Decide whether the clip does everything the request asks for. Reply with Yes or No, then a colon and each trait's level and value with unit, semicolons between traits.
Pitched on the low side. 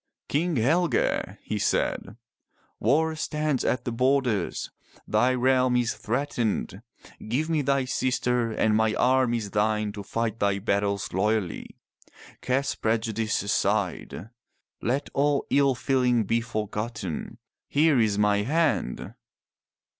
Yes: low, 120 Hz